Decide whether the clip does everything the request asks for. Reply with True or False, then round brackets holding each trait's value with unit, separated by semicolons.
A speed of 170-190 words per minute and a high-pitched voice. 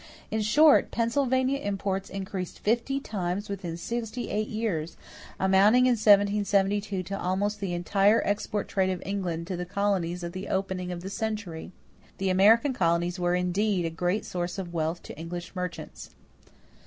False (155 wpm; 195 Hz)